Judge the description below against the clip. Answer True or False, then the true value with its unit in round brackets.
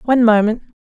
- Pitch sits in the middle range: False (225 Hz)